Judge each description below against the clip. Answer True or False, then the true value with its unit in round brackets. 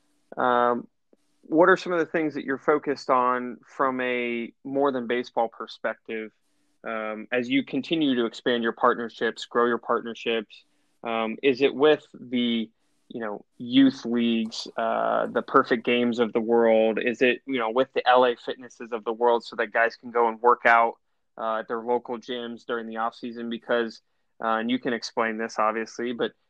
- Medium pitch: False (120 Hz)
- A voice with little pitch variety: True (2.0 semitones)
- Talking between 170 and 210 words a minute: True (185 wpm)